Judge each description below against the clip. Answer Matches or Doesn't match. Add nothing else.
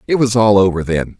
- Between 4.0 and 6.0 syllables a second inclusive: Matches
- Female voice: Doesn't match